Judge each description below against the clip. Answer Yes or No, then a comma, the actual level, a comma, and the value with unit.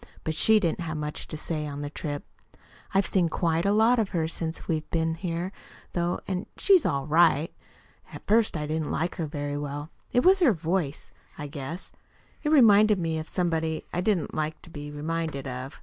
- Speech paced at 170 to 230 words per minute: Yes, average, 195 wpm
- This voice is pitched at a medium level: Yes, medium, 165 Hz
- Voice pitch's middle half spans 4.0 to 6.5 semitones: No, average, 3.5 semitones